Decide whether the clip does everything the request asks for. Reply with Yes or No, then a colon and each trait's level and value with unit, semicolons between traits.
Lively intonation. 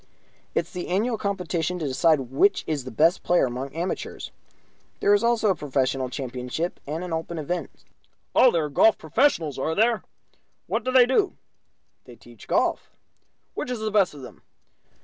Yes: wide, 6.5 semitones